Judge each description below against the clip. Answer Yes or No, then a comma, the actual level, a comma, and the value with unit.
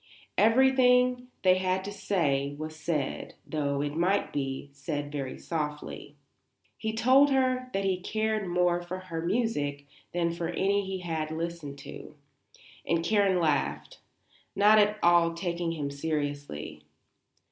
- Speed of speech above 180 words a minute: No, slow, 135 wpm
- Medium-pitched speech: Yes, medium, 170 Hz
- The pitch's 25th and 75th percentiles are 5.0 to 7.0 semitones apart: Yes, average, 5.3 semitones